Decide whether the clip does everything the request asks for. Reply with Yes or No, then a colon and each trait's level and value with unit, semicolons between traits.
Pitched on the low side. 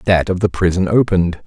Yes: very low, 90 Hz